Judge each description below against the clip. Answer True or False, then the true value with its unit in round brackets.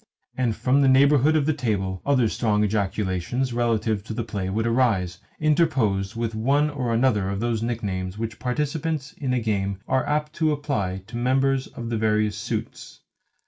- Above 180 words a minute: False (175 wpm)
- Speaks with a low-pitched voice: True (115 Hz)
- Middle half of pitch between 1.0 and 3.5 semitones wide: False (4.5 semitones)